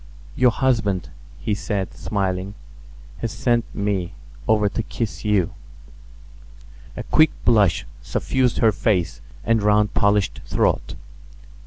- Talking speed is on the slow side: Yes, slow, 115 wpm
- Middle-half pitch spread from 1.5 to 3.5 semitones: Yes, average, 2.7 semitones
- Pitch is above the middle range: No, low, 105 Hz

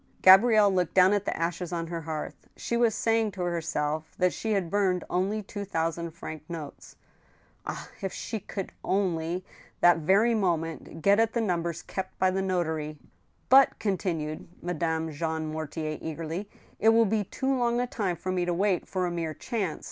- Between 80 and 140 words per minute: No, average, 180 wpm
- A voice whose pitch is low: No, medium, 180 Hz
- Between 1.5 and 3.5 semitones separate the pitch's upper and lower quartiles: No, average, 3.9 semitones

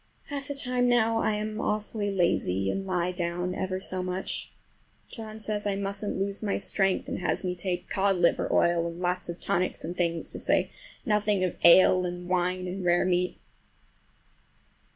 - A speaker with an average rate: Yes, average, 175 wpm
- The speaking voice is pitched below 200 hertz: Yes, medium, 185 Hz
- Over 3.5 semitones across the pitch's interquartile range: No, average, 2.7 semitones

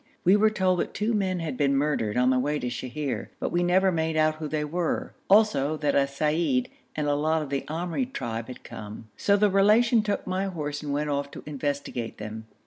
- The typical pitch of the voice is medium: Yes, medium, 150 Hz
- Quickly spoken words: Yes, fast, 225 wpm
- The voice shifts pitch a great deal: No, average, 5.0 semitones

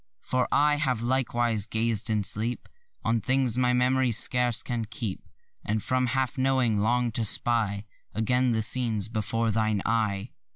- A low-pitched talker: Yes, low, 115 Hz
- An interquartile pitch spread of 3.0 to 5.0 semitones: No, narrow, 2.6 semitones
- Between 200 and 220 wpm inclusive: No, average, 155 wpm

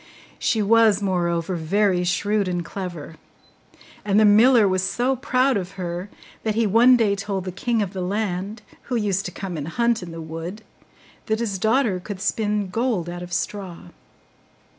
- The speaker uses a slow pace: No, average, 175 wpm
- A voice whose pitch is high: Yes, high, 200 Hz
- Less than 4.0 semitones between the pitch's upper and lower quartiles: Yes, average, 3.5 semitones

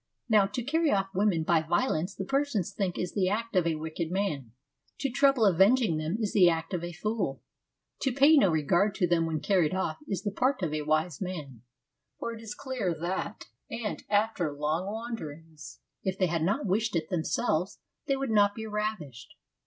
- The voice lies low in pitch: No, high, 190 Hz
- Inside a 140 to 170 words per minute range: No, average, 185 wpm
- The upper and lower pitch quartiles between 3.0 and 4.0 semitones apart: No, average, 5.2 semitones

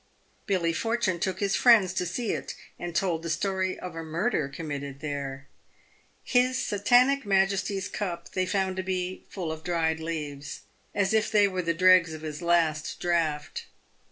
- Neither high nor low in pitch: Yes, medium, 180 Hz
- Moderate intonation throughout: Yes, average, 3.5 semitones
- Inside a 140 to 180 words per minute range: Yes, average, 165 wpm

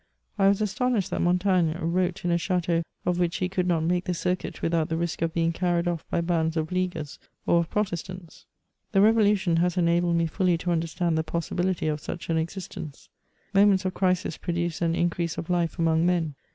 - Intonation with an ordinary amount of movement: No, narrow, 1.7 semitones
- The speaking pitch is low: No, medium, 175 Hz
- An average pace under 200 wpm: No, fast, 205 wpm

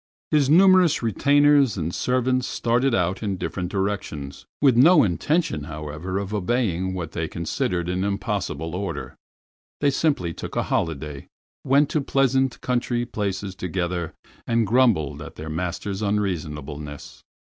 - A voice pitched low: Yes, low, 100 Hz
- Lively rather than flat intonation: Yes, wide, 7.1 semitones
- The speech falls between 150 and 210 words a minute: No, slow, 135 wpm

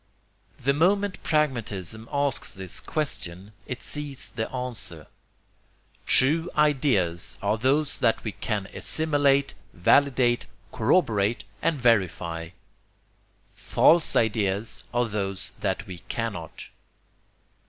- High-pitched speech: No, low, 120 Hz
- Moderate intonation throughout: No, wide, 6.4 semitones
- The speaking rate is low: Yes, slow, 100 wpm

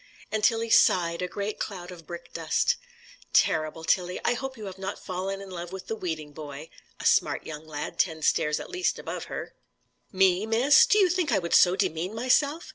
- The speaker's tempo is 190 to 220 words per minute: Yes, fast, 205 wpm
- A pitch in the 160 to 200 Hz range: Yes, medium, 185 Hz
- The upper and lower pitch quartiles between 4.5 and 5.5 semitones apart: Yes, average, 5.1 semitones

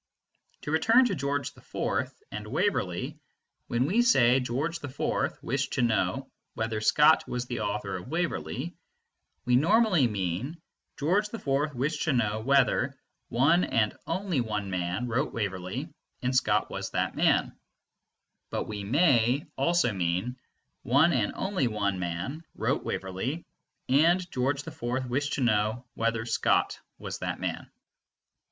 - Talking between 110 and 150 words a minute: Yes, average, 140 wpm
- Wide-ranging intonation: Yes, wide, 6.4 semitones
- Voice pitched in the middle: No, low, 125 Hz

